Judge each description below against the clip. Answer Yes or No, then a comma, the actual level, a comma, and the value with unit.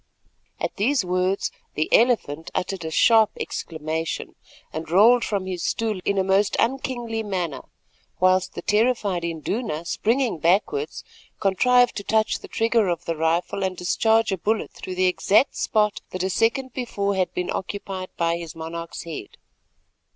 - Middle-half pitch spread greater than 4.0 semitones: Yes, average, 4.5 semitones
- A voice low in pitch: No, high, 195 Hz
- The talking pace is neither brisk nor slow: Yes, average, 155 wpm